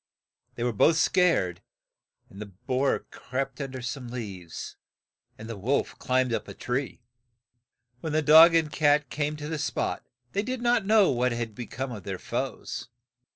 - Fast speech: No, average, 180 wpm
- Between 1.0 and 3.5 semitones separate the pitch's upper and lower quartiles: No, average, 4.6 semitones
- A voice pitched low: Yes, low, 130 Hz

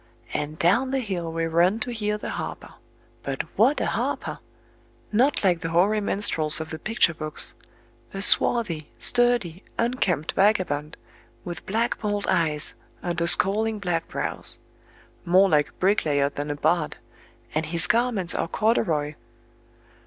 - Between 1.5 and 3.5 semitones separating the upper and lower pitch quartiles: No, average, 5.1 semitones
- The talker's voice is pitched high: No, medium, 175 Hz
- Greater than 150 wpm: No, average, 140 wpm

